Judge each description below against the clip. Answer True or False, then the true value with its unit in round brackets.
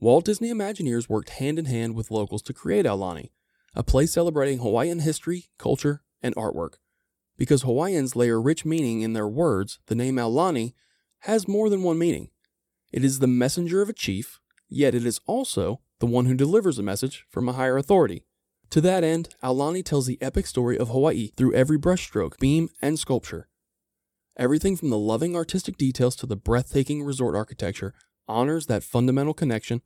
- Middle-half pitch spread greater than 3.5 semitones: True (5.5 semitones)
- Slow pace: False (175 wpm)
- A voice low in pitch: True (130 Hz)